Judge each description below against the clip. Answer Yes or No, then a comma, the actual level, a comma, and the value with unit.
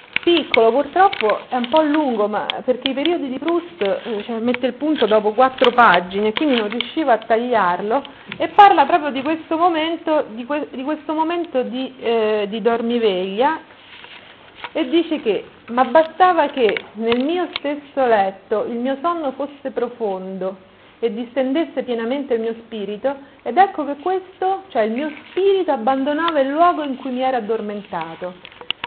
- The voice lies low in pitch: No, very high, 265 Hz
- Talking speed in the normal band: Yes, average, 160 wpm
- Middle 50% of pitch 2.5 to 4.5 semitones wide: No, wide, 5.4 semitones